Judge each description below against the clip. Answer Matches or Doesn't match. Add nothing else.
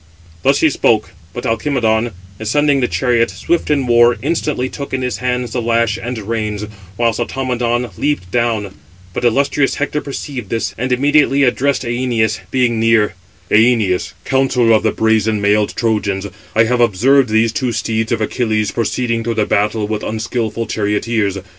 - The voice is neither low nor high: Doesn't match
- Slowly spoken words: Doesn't match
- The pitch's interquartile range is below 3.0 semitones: Matches